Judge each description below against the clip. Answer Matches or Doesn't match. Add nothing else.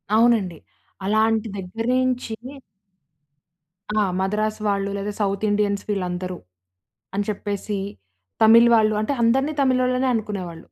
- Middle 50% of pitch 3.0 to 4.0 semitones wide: Doesn't match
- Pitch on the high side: Matches